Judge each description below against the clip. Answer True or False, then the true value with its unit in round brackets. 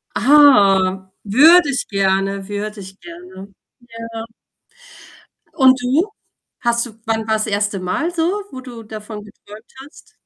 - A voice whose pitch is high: True (215 Hz)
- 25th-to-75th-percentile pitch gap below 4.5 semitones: False (4.8 semitones)